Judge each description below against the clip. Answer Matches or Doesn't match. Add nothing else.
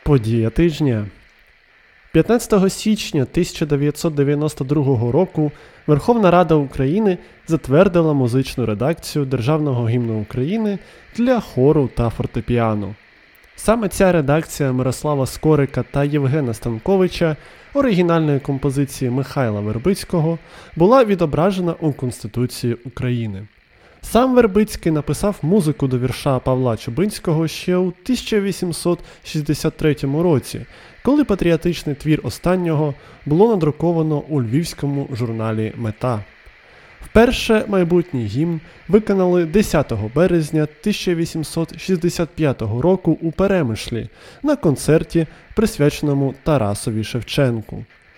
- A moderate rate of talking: Doesn't match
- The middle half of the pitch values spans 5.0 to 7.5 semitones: Matches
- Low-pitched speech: Doesn't match